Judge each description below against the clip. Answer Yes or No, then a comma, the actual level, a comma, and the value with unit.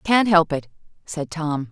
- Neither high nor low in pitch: Yes, medium, 165 Hz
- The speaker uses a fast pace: No, average, 175 wpm